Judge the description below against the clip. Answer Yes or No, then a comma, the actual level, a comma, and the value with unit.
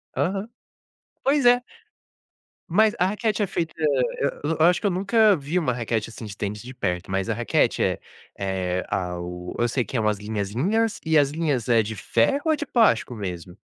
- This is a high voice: No, low, 125 Hz